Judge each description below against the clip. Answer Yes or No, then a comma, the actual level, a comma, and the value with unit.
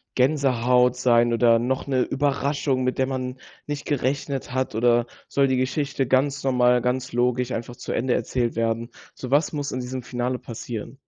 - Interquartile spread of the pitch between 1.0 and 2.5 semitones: Yes, narrow, 1.8 semitones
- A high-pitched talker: No, low, 125 Hz